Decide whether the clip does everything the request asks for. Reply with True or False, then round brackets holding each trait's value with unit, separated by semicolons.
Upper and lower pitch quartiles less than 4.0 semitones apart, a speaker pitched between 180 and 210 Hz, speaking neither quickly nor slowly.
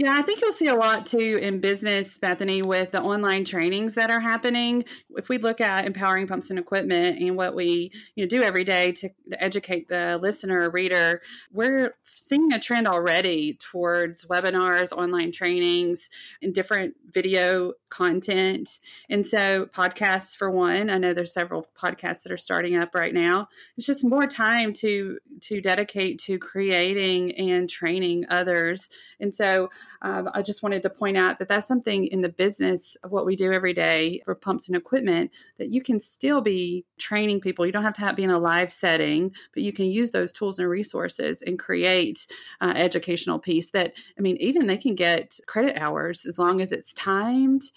True (2.9 semitones; 190 Hz; 185 wpm)